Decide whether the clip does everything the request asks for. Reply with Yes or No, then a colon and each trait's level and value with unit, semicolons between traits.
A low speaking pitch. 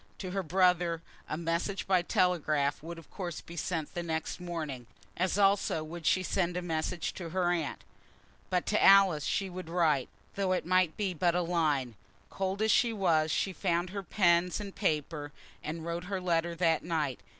No: medium, 175 Hz